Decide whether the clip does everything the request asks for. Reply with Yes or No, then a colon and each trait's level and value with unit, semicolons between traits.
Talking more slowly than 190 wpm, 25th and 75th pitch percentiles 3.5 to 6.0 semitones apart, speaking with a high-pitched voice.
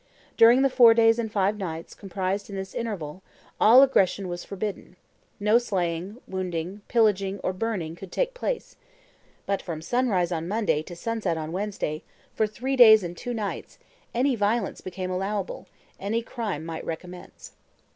Yes: average, 155 wpm; average, 4.1 semitones; high, 200 Hz